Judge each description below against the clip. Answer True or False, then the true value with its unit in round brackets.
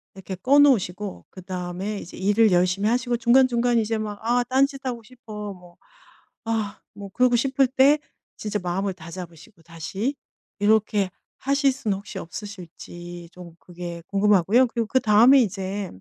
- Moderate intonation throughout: True (4.9 semitones)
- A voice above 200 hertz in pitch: True (210 Hz)